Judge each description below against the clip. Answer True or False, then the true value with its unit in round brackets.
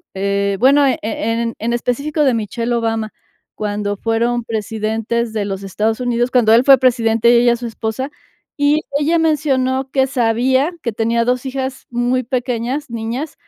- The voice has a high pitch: True (235 Hz)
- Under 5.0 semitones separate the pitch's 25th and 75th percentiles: True (2.6 semitones)